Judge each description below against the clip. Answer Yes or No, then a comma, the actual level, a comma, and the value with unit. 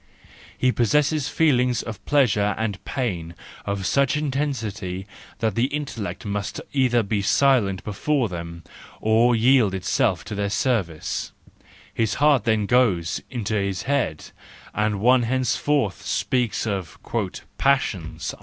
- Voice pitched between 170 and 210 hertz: No, low, 115 Hz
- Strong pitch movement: No, average, 4.8 semitones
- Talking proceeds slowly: Yes, slow, 125 wpm